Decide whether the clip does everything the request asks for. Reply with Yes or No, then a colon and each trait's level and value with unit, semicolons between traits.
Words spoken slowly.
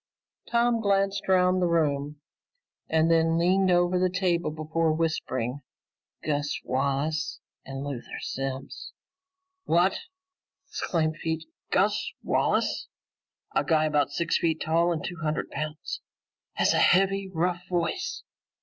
Yes: slow, 120 wpm